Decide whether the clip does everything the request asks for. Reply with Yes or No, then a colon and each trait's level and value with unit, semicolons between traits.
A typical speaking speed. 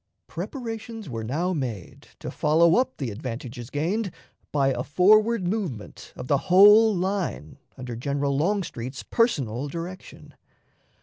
No: slow, 125 wpm